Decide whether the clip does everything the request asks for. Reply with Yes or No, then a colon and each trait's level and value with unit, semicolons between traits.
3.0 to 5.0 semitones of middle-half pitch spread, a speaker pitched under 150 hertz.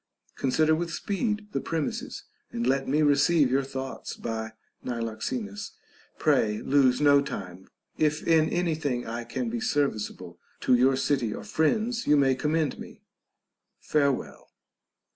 Yes: average, 4.4 semitones; medium, 140 Hz